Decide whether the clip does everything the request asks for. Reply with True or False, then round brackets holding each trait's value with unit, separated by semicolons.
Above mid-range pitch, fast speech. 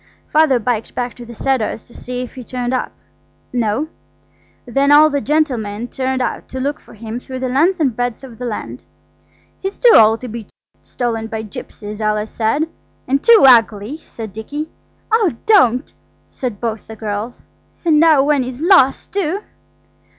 False (250 Hz; 170 wpm)